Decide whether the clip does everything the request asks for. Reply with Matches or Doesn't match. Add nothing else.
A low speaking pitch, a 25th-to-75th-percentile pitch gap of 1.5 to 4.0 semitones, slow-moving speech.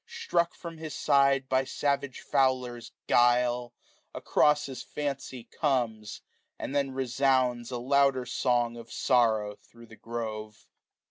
Matches